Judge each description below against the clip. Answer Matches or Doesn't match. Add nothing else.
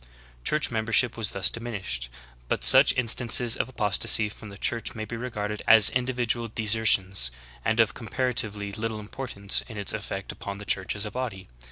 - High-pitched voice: Doesn't match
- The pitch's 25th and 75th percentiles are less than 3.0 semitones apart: Matches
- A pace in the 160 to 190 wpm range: Matches